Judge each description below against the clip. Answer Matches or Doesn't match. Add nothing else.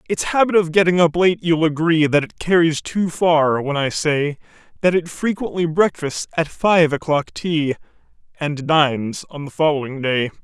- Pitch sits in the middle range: Matches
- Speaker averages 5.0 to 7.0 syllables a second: Doesn't match